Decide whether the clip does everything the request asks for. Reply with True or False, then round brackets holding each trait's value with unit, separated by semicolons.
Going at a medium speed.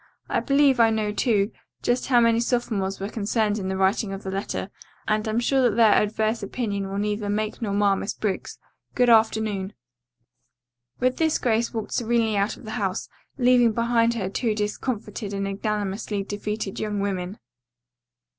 True (170 wpm)